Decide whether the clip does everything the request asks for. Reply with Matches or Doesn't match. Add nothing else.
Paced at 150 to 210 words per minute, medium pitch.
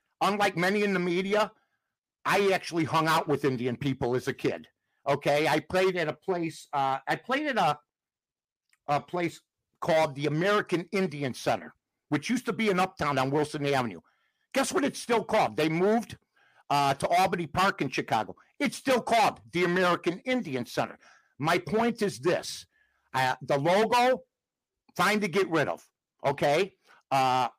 Matches